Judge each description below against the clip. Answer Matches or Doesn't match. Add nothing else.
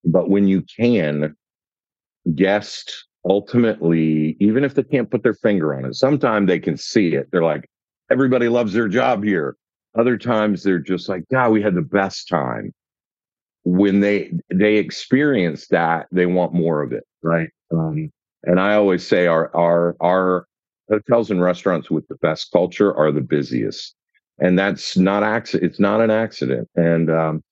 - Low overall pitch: Matches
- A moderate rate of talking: Matches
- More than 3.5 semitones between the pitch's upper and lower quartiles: Matches